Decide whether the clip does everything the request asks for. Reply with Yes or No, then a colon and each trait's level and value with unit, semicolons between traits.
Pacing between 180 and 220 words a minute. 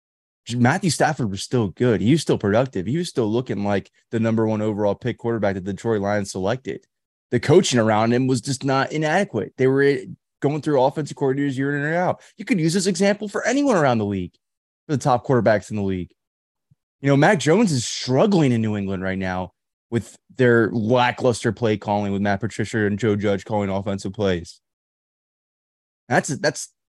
Yes: average, 195 wpm